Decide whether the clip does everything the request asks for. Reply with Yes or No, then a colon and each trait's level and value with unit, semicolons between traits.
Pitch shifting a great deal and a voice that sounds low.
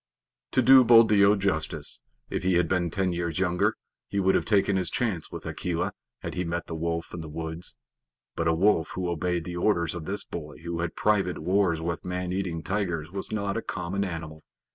No: average, 2.9 semitones; very low, 90 Hz